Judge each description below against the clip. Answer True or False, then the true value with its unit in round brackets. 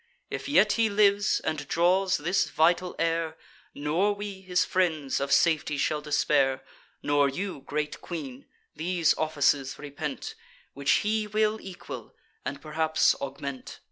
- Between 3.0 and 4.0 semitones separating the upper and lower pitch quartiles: False (4.7 semitones)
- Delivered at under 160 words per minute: True (135 wpm)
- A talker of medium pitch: True (160 Hz)